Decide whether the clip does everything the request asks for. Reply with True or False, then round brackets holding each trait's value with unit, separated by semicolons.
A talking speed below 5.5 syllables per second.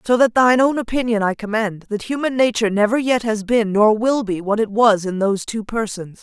False (5.6 syllables/s)